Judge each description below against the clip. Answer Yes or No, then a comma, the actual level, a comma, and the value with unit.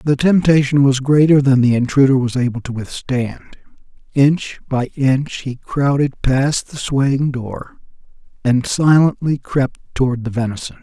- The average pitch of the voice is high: No, low, 135 Hz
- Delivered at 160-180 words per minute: No, average, 145 wpm